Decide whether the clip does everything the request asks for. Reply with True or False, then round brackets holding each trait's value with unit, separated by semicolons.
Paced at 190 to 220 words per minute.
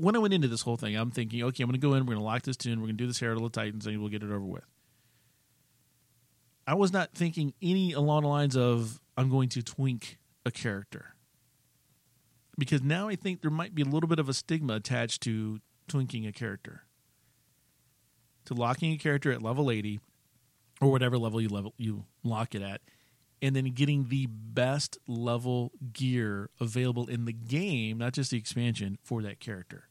True (205 wpm)